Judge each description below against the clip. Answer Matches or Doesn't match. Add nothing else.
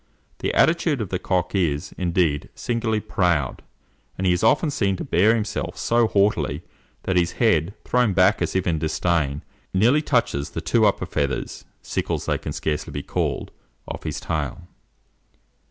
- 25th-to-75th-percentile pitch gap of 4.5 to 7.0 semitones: Matches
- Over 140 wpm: Matches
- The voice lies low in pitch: Matches